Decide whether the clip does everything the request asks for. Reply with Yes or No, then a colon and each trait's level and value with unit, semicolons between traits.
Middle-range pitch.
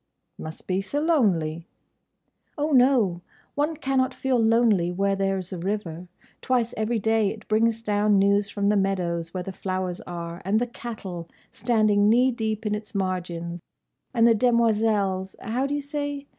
No: high, 210 Hz